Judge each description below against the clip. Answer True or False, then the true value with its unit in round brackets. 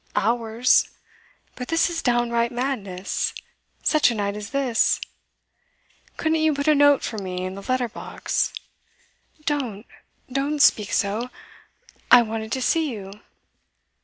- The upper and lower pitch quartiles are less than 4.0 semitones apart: False (4.9 semitones)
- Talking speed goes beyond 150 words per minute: False (135 wpm)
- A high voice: True (240 Hz)